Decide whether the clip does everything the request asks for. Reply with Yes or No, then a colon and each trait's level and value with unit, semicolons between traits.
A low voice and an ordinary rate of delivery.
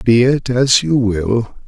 Yes: low, 120 Hz; average, 180 wpm